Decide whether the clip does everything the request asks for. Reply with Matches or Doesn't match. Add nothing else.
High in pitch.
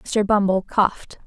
Matches